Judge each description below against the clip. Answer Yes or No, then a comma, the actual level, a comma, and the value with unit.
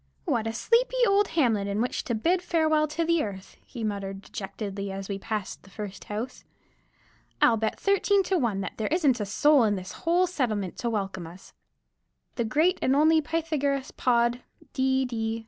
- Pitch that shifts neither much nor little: No, wide, 7.3 semitones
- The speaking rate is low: No, average, 180 wpm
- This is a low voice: No, high, 235 Hz